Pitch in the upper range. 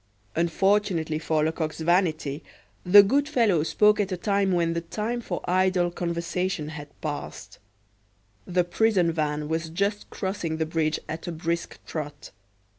No: medium, 170 Hz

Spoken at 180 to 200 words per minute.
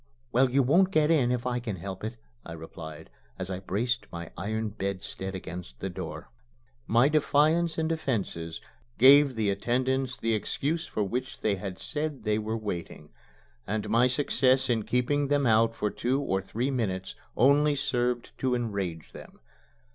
No: average, 165 wpm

